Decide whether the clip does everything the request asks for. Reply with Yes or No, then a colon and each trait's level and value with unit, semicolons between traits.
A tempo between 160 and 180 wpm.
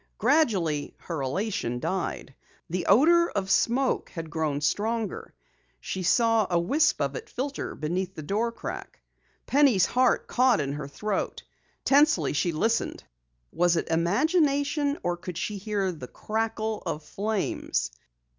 No: slow, 135 wpm